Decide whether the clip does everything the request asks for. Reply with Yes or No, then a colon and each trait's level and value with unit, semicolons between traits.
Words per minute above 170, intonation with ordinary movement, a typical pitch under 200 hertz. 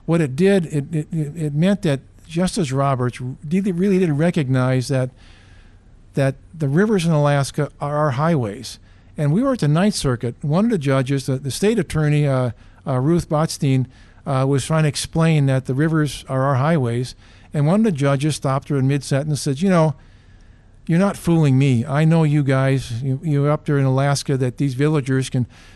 Yes: average, 195 wpm; average, 3.6 semitones; medium, 140 Hz